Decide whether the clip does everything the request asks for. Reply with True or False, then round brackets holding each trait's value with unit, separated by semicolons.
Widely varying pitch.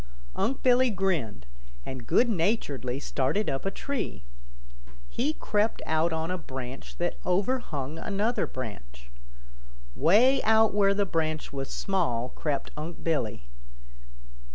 True (7.7 semitones)